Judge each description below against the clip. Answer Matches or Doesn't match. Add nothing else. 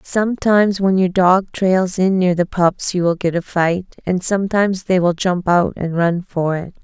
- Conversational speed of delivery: Doesn't match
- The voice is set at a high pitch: Doesn't match